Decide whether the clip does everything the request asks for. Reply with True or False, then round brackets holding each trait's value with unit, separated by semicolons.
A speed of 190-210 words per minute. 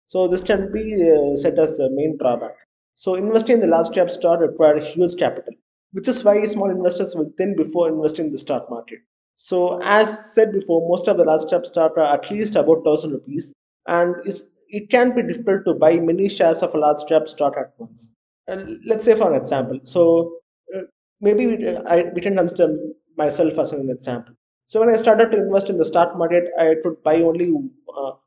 True (200 wpm)